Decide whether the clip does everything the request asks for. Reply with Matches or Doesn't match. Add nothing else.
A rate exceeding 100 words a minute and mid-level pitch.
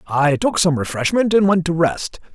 Matches